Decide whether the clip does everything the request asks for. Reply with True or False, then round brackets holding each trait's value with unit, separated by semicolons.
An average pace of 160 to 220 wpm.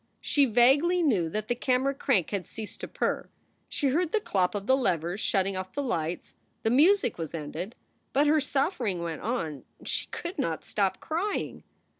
True (180 wpm)